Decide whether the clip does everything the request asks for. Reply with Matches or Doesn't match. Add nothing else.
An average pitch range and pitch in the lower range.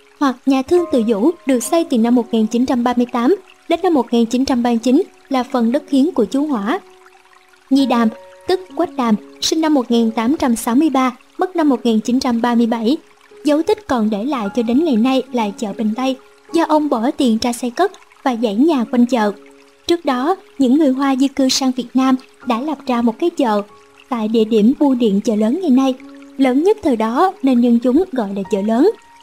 Doesn't match